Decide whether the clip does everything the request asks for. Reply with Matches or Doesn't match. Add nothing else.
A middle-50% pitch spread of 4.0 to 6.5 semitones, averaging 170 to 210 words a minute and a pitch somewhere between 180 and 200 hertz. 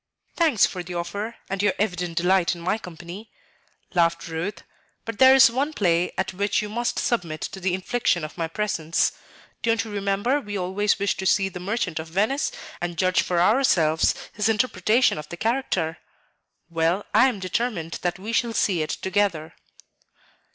Matches